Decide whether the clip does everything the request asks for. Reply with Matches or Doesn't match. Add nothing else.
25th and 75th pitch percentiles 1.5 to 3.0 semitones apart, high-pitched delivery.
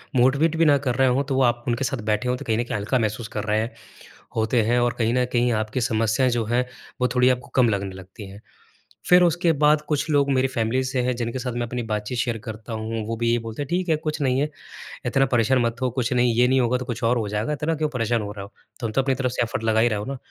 Doesn't match